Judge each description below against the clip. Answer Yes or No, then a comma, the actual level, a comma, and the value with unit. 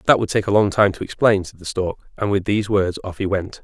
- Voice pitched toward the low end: Yes, low, 100 Hz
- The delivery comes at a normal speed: No, fast, 295 wpm